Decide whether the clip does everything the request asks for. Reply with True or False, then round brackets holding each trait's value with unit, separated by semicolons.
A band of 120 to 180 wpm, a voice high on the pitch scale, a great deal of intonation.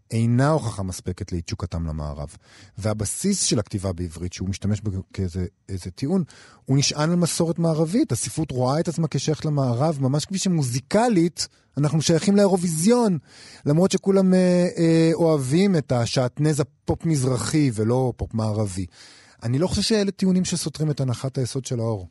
False (140 wpm; 135 Hz; 7.4 semitones)